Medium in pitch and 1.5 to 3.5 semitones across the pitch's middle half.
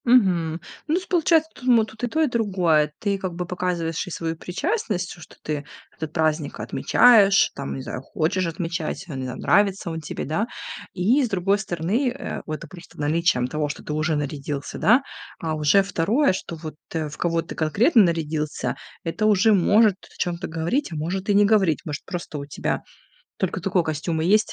No: medium, 175 Hz; average, 4.6 semitones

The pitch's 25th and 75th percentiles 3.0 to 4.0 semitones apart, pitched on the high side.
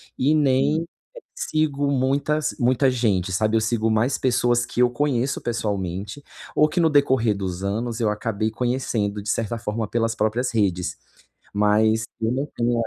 No: average, 3.6 semitones; low, 115 Hz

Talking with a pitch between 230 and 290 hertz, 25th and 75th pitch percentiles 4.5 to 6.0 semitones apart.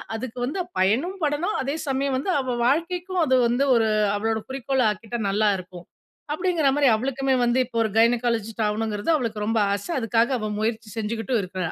No: high, 235 Hz; average, 3.9 semitones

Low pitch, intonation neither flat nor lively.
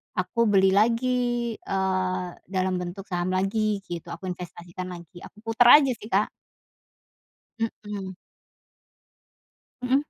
No: high, 195 Hz; average, 3.6 semitones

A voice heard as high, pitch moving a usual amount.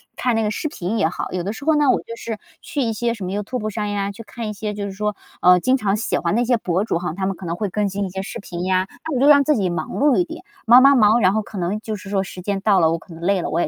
Yes: high, 205 Hz; average, 3.6 semitones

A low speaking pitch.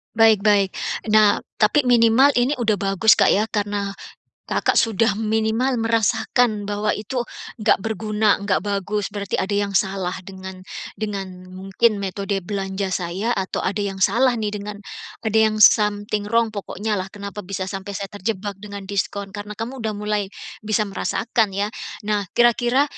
No: high, 205 Hz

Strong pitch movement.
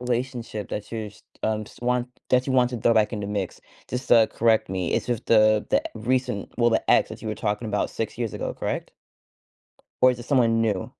No: narrow, 2.5 semitones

